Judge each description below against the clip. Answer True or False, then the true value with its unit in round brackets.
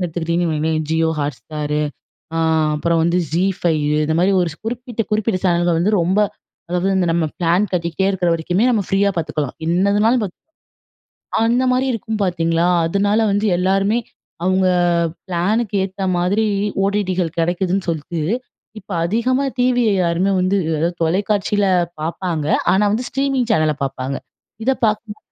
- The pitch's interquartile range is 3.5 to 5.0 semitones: True (3.8 semitones)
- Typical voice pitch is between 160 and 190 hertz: True (185 Hz)